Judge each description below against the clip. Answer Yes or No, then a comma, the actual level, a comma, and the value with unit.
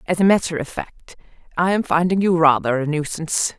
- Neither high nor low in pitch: Yes, medium, 165 Hz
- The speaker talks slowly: No, average, 200 wpm